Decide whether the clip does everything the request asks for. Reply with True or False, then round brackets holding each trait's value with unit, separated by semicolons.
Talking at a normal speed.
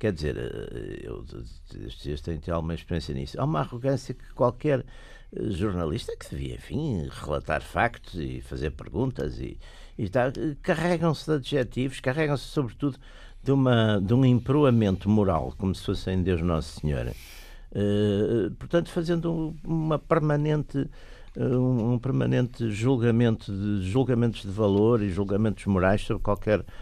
True (140 wpm)